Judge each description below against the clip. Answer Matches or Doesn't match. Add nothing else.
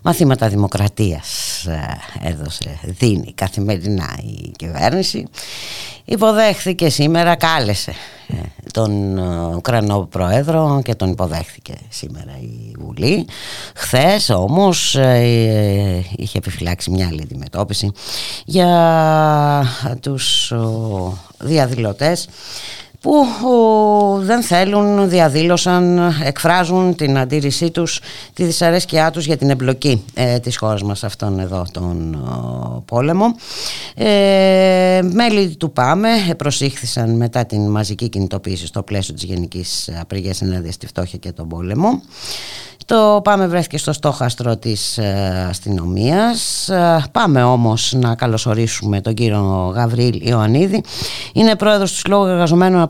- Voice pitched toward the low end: Matches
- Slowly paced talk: Matches